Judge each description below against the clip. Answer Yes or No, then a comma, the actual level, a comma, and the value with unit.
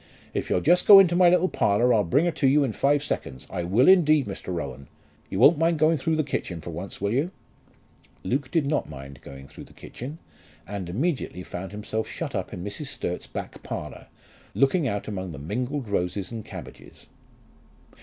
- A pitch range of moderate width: No, wide, 8.5 semitones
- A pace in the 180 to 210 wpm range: Yes, average, 200 wpm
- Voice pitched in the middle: No, low, 120 Hz